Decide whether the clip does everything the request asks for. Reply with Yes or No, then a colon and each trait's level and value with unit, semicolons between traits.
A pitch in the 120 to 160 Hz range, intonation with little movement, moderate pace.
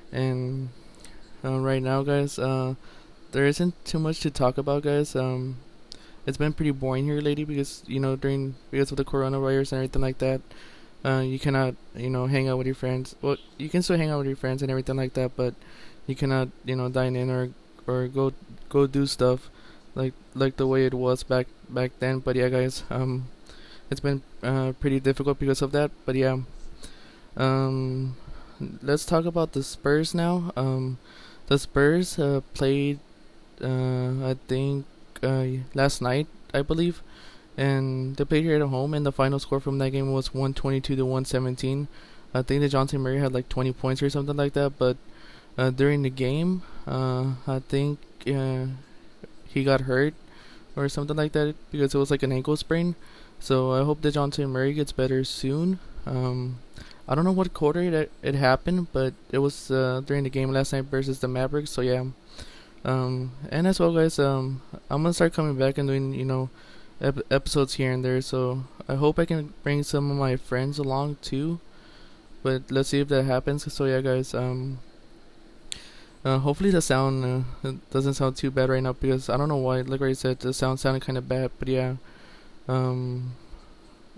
Yes: low, 135 Hz; narrow, 1.6 semitones; average, 190 wpm